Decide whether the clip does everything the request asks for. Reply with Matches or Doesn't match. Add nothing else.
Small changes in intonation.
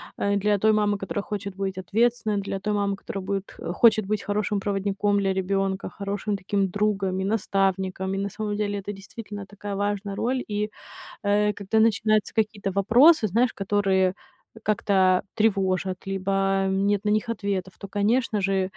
Matches